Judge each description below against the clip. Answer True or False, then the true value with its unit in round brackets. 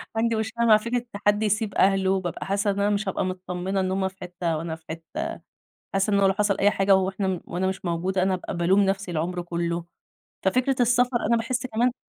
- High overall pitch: True (195 Hz)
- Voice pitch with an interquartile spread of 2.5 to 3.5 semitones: True (2.9 semitones)